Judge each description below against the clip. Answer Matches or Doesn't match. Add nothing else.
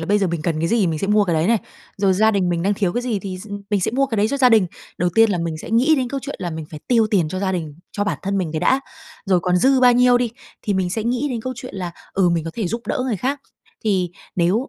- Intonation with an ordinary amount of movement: Matches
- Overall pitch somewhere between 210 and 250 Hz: Doesn't match